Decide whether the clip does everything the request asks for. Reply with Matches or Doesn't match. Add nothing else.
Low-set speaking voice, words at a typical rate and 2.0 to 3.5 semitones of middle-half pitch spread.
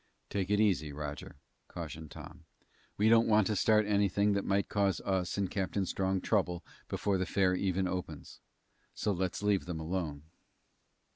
Matches